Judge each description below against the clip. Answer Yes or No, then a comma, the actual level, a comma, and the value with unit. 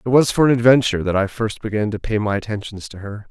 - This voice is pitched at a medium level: No, low, 110 Hz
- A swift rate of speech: Yes, fast, 275 wpm